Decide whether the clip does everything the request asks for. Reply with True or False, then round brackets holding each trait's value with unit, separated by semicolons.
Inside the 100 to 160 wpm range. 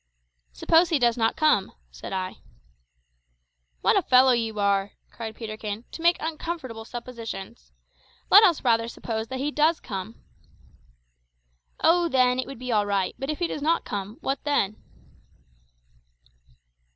True (145 wpm)